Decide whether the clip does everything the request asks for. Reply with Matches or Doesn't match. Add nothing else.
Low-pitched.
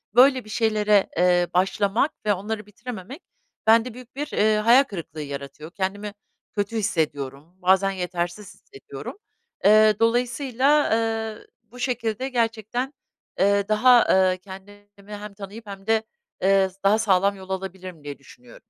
Doesn't match